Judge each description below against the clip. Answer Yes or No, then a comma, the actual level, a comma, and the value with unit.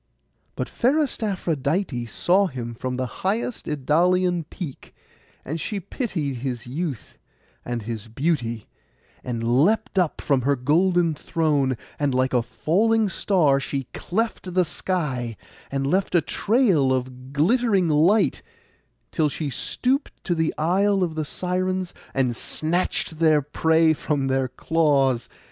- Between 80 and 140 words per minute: Yes, slow, 135 wpm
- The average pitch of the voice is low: No, medium, 155 Hz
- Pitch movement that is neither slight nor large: No, wide, 5.9 semitones